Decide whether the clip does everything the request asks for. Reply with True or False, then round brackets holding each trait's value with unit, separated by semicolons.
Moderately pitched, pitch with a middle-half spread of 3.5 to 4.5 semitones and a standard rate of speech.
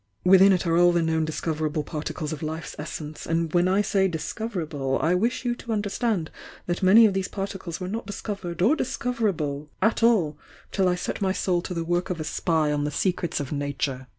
False (175 Hz; 4.1 semitones; 215 wpm)